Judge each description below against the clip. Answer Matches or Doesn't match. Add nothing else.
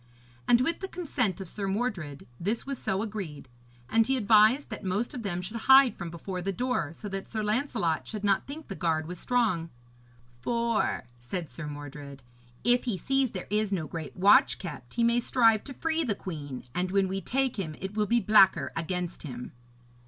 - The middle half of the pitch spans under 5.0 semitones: Doesn't match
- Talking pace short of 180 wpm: Doesn't match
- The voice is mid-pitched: Doesn't match